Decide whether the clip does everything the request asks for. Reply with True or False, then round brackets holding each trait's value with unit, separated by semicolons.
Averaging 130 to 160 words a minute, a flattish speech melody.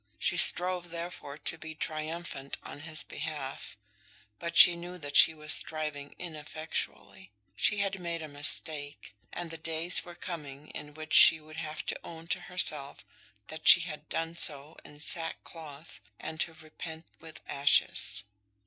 True (155 wpm; 2.2 semitones)